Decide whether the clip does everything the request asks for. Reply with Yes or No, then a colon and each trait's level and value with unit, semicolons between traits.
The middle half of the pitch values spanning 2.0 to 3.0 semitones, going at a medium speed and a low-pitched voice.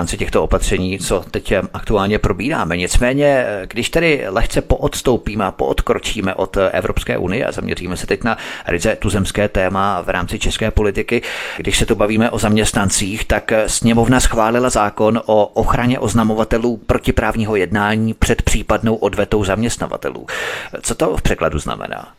Yes: average, 2.7 semitones; average, 140 wpm; low, 110 Hz